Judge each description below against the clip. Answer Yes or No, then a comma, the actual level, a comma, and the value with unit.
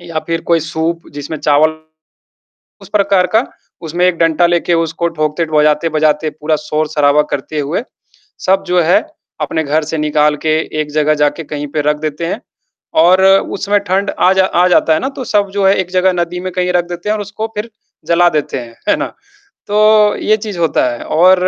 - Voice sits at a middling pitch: Yes, medium, 170 Hz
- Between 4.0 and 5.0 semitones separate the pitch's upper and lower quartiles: No, average, 3.6 semitones